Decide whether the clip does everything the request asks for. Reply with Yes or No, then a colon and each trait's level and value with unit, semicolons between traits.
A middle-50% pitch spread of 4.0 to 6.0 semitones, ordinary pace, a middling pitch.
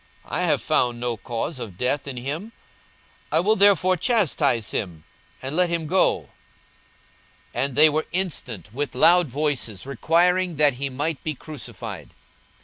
Yes: wide, 5.6 semitones; average, 150 wpm; medium, 145 Hz